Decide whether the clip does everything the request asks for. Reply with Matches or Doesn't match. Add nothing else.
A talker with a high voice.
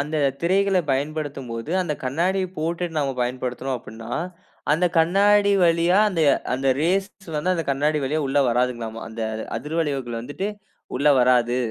Doesn't match